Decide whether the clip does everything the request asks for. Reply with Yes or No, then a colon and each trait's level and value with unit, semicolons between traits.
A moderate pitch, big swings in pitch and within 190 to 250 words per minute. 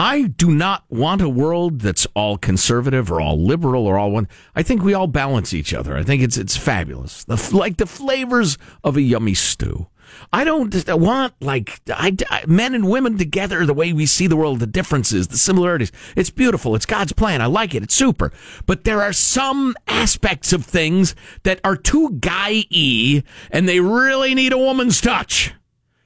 Yes: medium, 165 Hz; wide, 8.9 semitones; average, 195 wpm